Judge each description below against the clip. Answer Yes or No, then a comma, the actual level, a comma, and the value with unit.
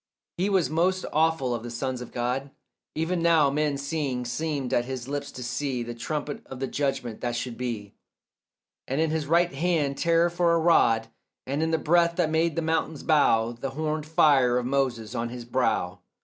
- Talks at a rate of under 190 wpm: No, average, 195 wpm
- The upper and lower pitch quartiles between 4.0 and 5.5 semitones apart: Yes, average, 4.6 semitones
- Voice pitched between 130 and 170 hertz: Yes, medium, 140 Hz